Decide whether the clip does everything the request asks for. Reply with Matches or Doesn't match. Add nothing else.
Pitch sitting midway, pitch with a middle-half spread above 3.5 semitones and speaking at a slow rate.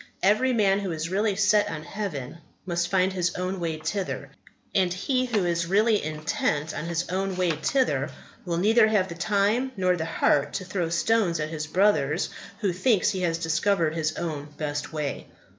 Doesn't match